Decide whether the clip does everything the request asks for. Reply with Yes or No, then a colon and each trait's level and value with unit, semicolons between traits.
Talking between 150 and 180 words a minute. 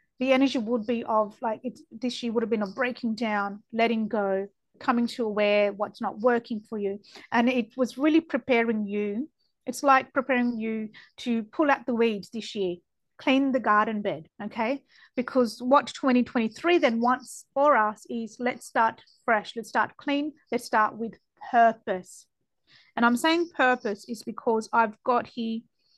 Yes: average, 170 wpm